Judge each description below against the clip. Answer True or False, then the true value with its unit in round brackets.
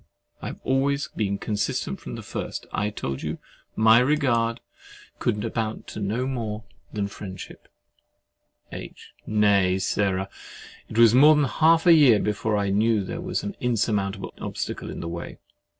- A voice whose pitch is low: True (110 Hz)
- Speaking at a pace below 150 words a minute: False (160 wpm)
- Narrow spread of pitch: False (4.2 semitones)